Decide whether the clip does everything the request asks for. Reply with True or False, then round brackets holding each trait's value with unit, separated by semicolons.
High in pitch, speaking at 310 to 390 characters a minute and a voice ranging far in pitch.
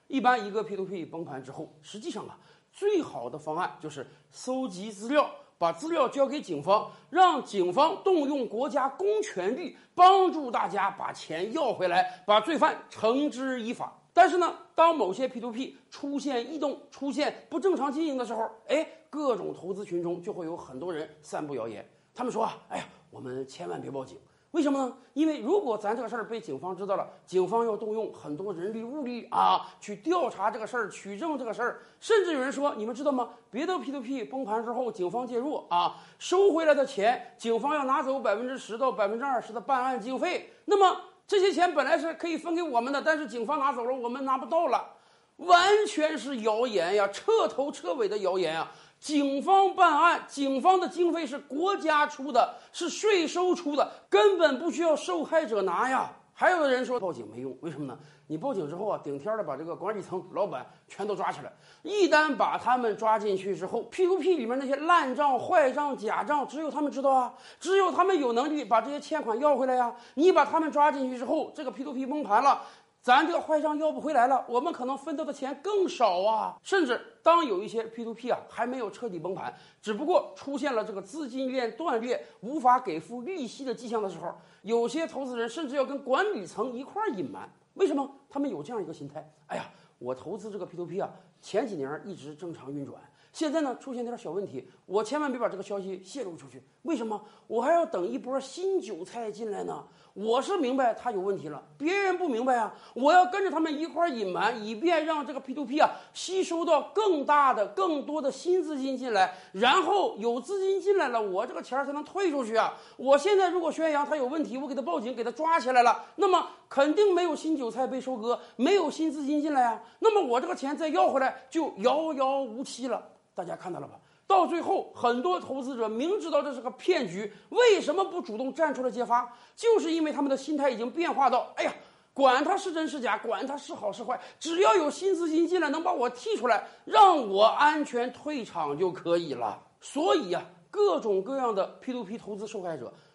True (275 Hz; 315 characters per minute; 6.2 semitones)